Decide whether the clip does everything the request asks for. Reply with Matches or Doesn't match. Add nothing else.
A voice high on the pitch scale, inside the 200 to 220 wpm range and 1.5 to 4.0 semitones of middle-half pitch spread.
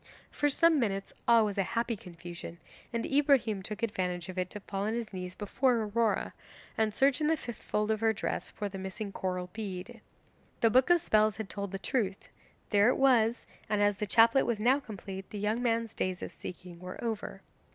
Matches